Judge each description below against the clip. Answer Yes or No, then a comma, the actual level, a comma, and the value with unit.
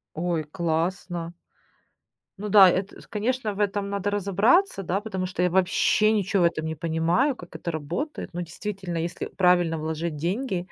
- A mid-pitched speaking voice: Yes, medium, 180 Hz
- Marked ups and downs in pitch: No, average, 3.3 semitones